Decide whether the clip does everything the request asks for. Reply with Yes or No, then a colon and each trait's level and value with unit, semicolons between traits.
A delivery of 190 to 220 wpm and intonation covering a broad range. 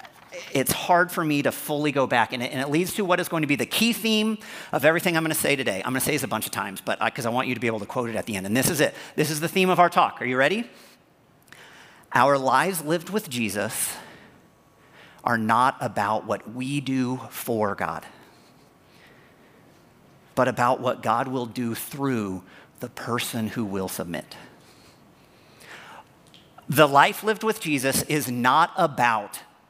Yes: average, 200 wpm; wide, 6.0 semitones